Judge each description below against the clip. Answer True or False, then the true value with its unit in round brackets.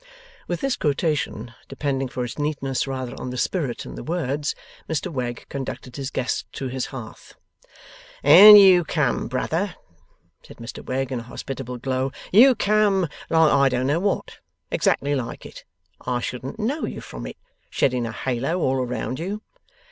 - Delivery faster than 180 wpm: False (165 wpm)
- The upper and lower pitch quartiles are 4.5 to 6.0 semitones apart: True (4.9 semitones)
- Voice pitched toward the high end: False (135 Hz)